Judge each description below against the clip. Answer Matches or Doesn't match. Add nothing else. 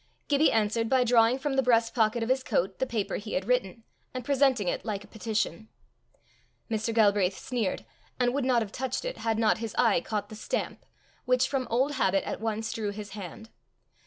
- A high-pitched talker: Matches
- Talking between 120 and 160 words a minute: Doesn't match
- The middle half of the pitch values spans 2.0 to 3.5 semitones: Matches